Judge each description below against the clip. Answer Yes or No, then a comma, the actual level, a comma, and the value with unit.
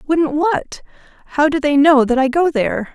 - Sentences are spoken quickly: No, average, 185 wpm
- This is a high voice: Yes, very high, 285 Hz